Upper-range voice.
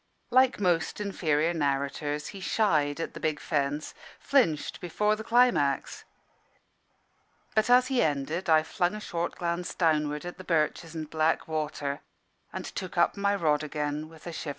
No: medium, 160 Hz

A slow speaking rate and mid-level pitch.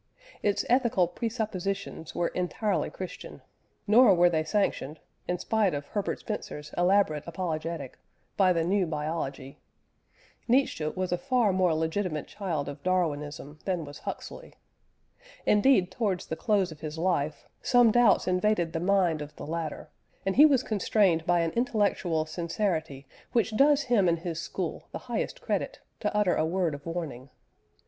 No: average, 155 wpm; medium, 180 Hz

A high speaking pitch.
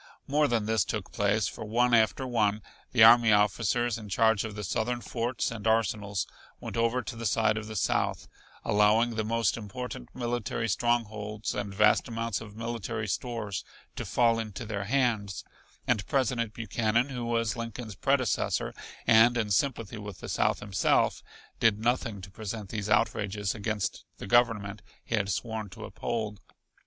No: low, 110 Hz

